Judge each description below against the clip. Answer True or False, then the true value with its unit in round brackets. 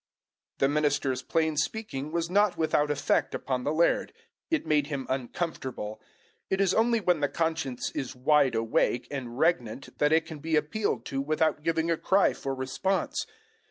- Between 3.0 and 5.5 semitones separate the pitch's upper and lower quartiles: True (3.7 semitones)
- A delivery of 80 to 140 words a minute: False (165 wpm)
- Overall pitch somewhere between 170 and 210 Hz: False (150 Hz)